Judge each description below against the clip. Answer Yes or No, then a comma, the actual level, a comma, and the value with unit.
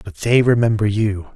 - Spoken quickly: No, average, 180 wpm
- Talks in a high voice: No, low, 105 Hz